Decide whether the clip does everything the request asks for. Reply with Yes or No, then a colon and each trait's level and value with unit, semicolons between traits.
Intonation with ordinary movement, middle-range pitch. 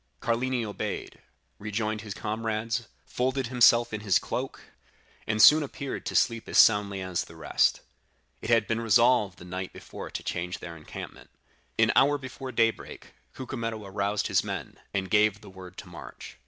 No: average, 3.1 semitones; low, 110 Hz